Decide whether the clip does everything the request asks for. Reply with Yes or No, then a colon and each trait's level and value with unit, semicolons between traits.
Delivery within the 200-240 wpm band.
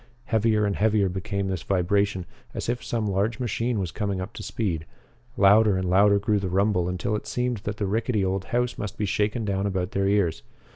Yes: fast, 205 wpm